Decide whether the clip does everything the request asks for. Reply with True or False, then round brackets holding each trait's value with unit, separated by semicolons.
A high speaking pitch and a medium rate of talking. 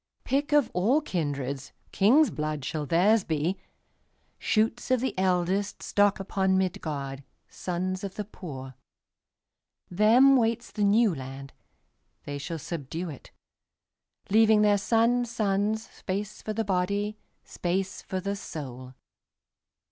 False (195 Hz; 95 wpm)